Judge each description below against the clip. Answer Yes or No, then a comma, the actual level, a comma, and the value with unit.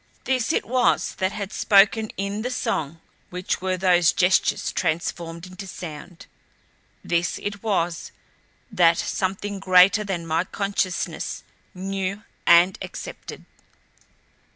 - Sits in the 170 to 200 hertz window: Yes, medium, 185 Hz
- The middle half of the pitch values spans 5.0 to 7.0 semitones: No, narrow, 2.6 semitones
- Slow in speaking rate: Yes, slow, 115 wpm